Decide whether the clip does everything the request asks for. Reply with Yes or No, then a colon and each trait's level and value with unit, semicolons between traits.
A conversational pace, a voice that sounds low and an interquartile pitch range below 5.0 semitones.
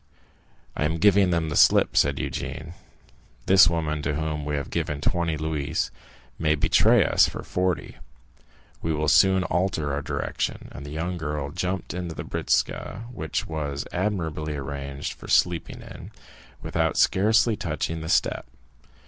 Yes: average, 150 wpm; very low, 80 Hz; average, 3.2 semitones